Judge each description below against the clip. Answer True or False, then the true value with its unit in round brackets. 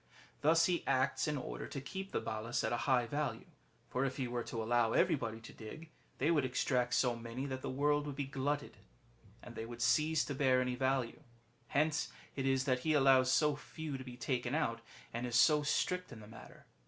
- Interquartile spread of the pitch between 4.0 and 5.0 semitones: False (3.4 semitones)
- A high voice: False (130 Hz)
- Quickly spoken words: True (220 wpm)